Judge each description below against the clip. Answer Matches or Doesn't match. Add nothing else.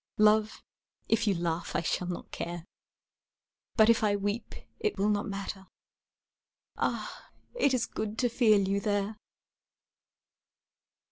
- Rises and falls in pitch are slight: Matches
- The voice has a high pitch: Matches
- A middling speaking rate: Doesn't match